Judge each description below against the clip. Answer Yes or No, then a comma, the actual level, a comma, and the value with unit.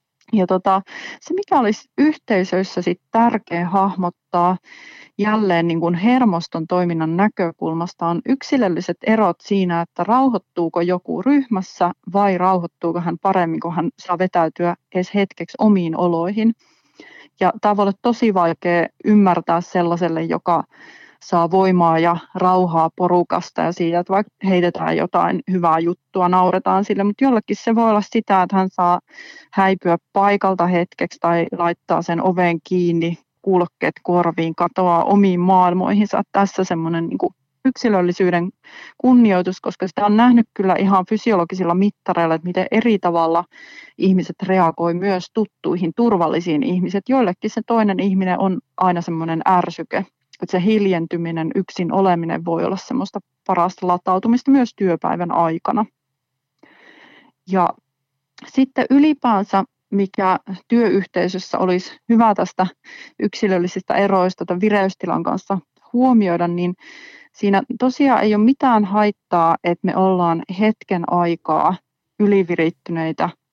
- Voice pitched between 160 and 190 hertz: Yes, medium, 185 Hz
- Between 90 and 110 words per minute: No, average, 125 wpm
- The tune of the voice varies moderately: Yes, average, 3.5 semitones